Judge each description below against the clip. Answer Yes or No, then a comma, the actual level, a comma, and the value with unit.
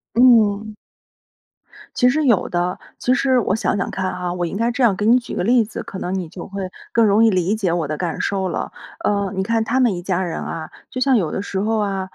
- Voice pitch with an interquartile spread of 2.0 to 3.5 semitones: No, average, 3.9 semitones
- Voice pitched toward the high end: Yes, high, 200 Hz